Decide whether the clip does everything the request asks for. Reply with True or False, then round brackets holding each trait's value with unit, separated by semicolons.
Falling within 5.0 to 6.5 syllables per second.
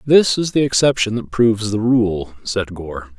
False (4.5 syllables/s)